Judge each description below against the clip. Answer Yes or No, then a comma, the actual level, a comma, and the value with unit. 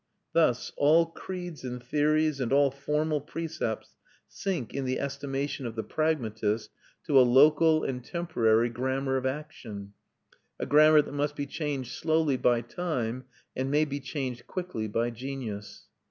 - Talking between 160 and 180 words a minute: No, average, 150 wpm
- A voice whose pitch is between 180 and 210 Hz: No, medium, 140 Hz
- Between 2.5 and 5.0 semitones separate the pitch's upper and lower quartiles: Yes, average, 3.9 semitones